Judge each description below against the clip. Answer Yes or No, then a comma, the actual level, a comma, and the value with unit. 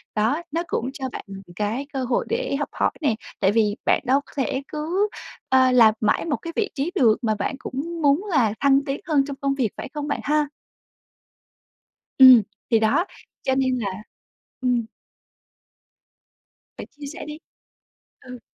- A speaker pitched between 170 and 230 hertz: No, very high, 270 Hz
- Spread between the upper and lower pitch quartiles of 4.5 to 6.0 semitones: No, average, 3.8 semitones